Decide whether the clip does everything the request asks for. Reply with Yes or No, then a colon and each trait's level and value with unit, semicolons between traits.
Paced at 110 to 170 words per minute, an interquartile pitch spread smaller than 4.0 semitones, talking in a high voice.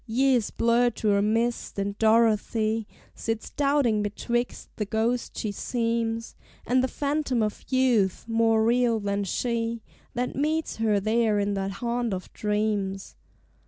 Yes: average, 140 wpm; narrow, 2.4 semitones; high, 225 Hz